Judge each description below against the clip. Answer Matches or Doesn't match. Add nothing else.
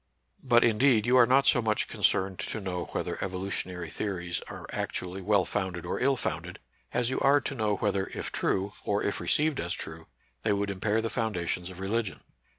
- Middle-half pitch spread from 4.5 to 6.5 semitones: Doesn't match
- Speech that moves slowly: Doesn't match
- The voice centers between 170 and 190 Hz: Doesn't match